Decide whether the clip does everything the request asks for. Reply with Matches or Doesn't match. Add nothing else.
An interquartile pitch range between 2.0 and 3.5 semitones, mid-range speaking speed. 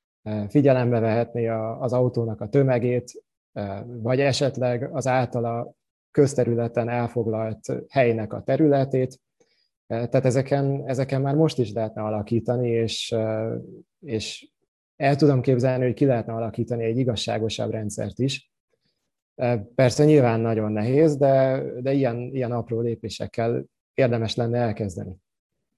Doesn't match